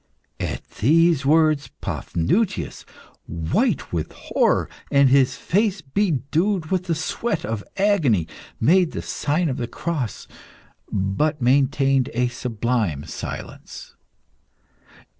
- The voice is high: No, medium, 140 Hz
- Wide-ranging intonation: Yes, wide, 6.0 semitones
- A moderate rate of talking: No, slow, 105 wpm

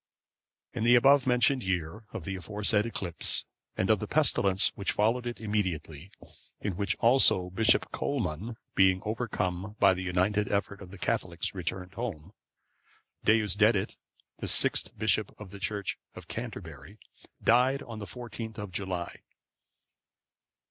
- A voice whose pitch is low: Yes, low, 105 Hz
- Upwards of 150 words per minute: No, average, 140 wpm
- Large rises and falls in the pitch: No, average, 3.5 semitones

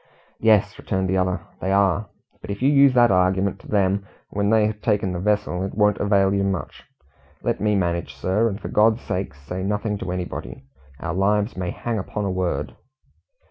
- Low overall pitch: Yes, low, 100 Hz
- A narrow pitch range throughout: Yes, narrow, 2.2 semitones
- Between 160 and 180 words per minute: No, average, 195 wpm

